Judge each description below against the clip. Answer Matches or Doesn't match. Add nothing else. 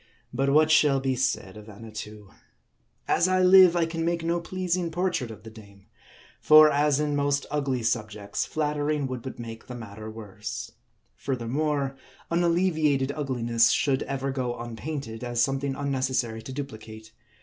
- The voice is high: Doesn't match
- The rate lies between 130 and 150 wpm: Doesn't match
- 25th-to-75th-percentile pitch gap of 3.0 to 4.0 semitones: Doesn't match